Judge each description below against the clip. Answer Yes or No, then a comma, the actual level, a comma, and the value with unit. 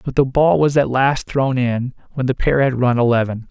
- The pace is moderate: No, fast, 225 wpm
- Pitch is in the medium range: No, low, 130 Hz